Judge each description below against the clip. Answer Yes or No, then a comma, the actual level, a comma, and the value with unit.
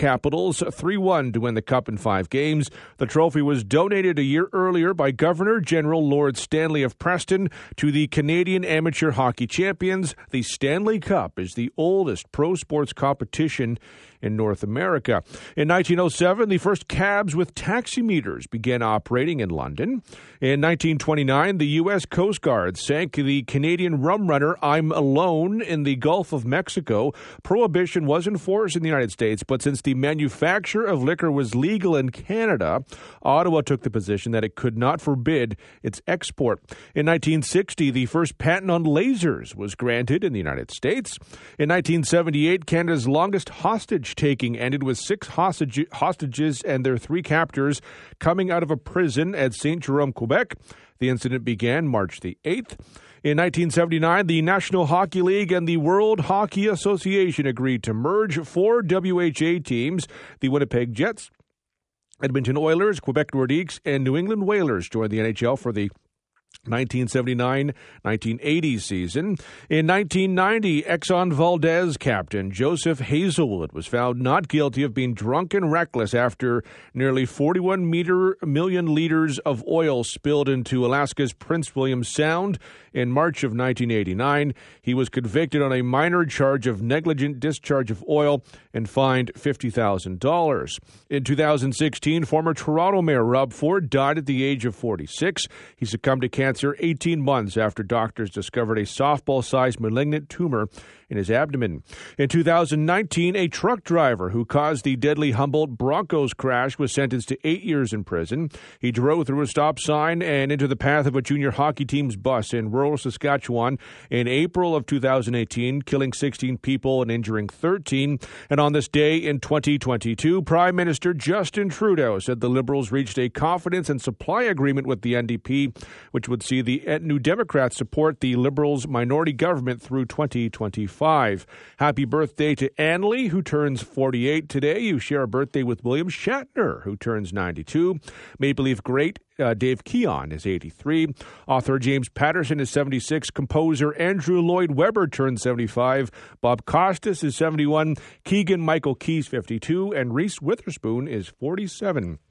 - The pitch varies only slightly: No, average, 4.7 semitones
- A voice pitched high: No, medium, 145 Hz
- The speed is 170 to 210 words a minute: No, average, 155 wpm